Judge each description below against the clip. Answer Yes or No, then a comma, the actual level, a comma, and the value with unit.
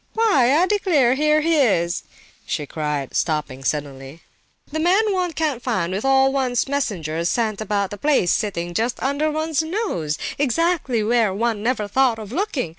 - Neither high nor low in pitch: No, high, 245 Hz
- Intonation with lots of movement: Yes, wide, 8.6 semitones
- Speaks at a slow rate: No, average, 165 wpm